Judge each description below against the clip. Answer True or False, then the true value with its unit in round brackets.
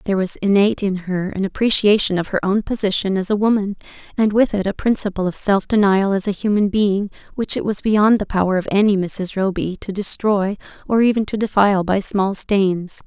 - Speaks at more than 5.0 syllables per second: True (5.5 syllables/s)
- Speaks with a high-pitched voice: True (200 Hz)